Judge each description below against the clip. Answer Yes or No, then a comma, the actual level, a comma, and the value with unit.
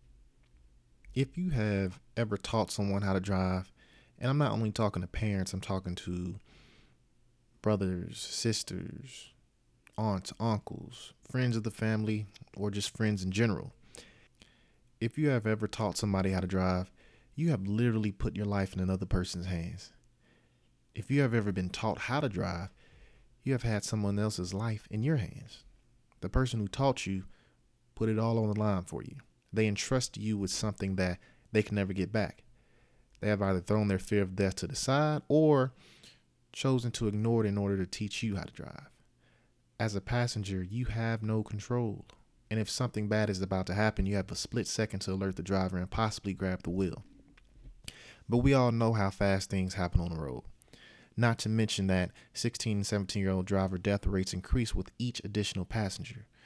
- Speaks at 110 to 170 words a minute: No, average, 185 wpm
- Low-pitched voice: Yes, low, 105 Hz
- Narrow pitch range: No, average, 3.4 semitones